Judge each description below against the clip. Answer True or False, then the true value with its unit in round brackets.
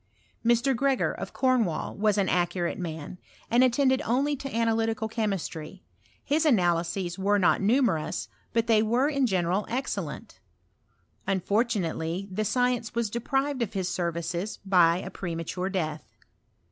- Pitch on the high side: True (205 Hz)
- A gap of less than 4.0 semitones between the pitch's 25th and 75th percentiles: False (5.3 semitones)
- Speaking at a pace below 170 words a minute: True (135 wpm)